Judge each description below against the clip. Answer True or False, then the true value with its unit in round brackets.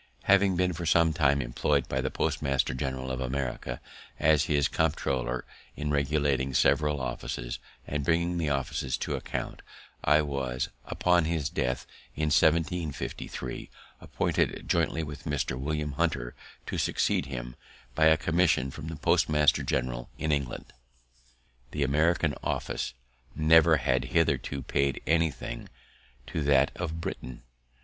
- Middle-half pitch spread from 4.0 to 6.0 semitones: False (3.3 semitones)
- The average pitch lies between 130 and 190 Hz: False (75 Hz)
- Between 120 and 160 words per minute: True (135 wpm)